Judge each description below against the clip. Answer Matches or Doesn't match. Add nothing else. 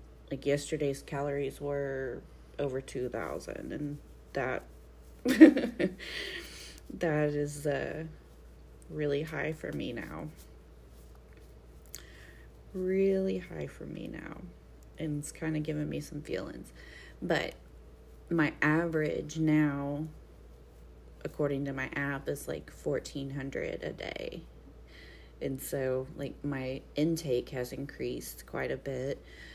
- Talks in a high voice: Doesn't match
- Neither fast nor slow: Doesn't match